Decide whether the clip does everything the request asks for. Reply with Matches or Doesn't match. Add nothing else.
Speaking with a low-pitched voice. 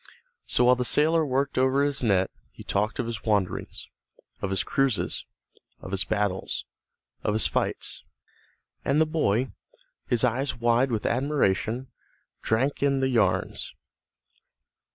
Matches